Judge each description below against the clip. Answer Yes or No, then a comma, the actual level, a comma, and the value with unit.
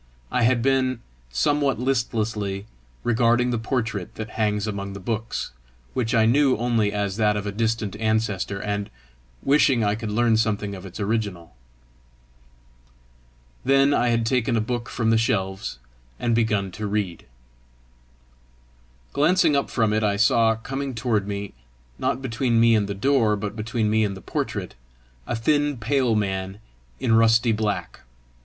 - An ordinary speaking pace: Yes, average, 155 wpm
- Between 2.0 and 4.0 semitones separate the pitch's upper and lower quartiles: Yes, average, 2.7 semitones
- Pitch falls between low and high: No, low, 110 Hz